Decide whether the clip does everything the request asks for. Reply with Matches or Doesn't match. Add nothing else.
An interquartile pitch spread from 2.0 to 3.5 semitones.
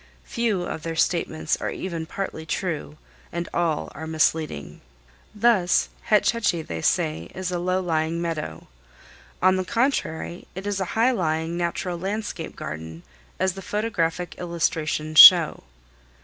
Matches